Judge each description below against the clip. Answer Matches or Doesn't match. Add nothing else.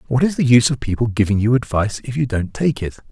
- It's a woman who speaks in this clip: Doesn't match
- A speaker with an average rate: Doesn't match